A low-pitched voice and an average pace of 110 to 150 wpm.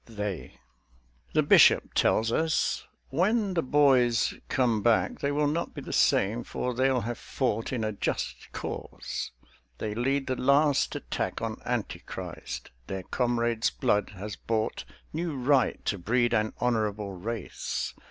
Yes: low, 120 Hz; average, 145 wpm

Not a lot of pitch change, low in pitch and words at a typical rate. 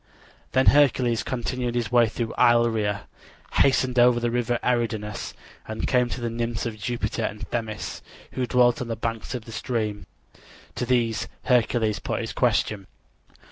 Yes: narrow, 1.9 semitones; low, 120 Hz; average, 155 wpm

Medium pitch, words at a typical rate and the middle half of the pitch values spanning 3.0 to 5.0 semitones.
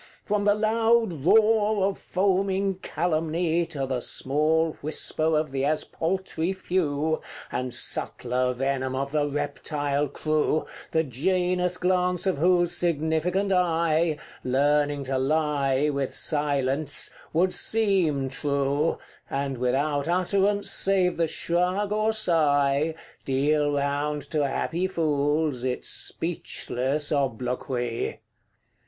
No: medium, 155 Hz; slow, 110 wpm; average, 4.3 semitones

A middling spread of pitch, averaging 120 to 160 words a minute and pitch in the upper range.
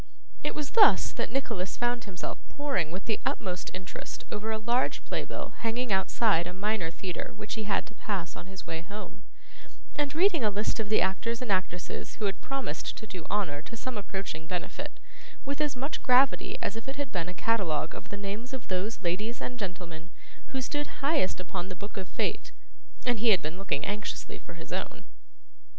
No: average, 4.7 semitones; average, 200 wpm; high, 210 Hz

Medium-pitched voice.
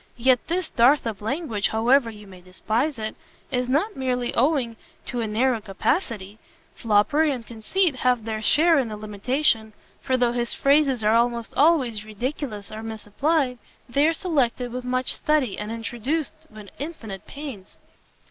No: high, 245 Hz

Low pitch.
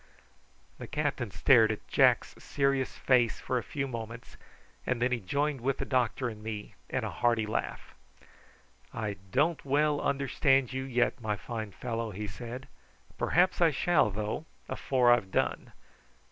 Yes: low, 125 Hz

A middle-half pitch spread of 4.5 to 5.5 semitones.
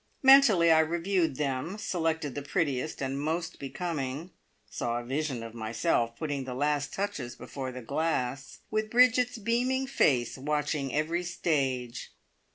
Yes: average, 5.0 semitones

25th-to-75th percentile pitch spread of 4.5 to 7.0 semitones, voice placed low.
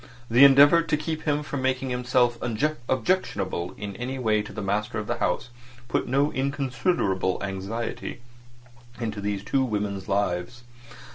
Yes: average, 4.8 semitones; low, 120 Hz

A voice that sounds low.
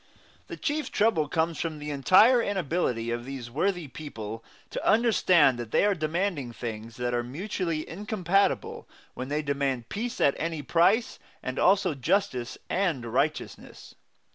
No: medium, 155 Hz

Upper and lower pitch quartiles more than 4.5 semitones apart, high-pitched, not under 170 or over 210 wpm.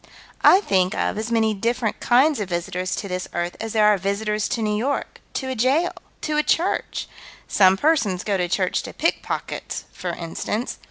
Yes: average, 5.0 semitones; high, 210 Hz; average, 195 wpm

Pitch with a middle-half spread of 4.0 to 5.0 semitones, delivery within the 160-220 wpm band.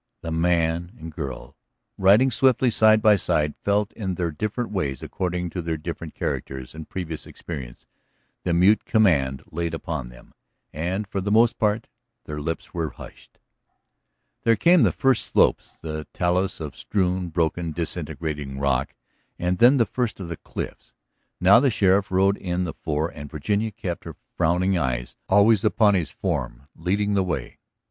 Yes: average, 4.6 semitones; average, 165 wpm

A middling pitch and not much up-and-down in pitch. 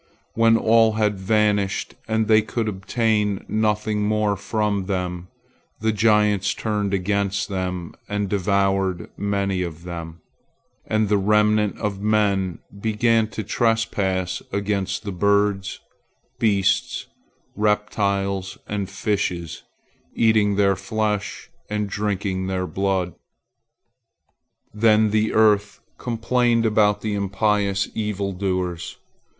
No: low, 105 Hz; narrow, 1.8 semitones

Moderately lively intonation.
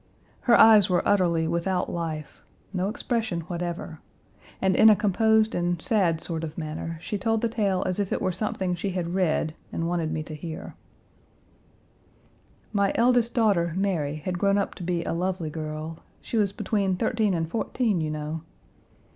Yes: average, 3.7 semitones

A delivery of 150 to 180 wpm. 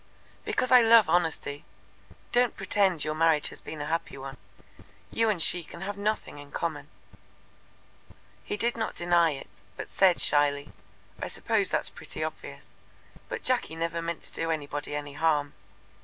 Yes: average, 160 wpm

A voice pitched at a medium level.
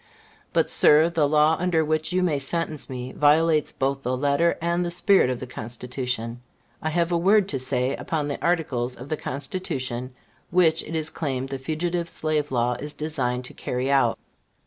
Yes: medium, 150 Hz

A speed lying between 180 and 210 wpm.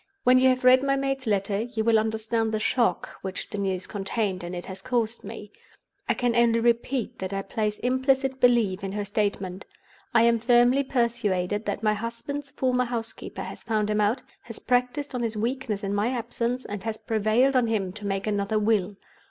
Yes: average, 195 wpm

